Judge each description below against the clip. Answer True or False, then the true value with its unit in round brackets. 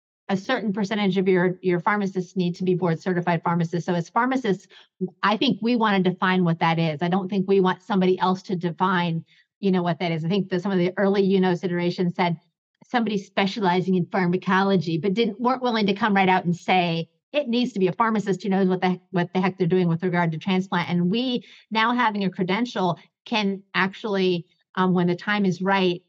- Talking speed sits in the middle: False (225 wpm)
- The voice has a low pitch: False (185 Hz)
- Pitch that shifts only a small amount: True (2.1 semitones)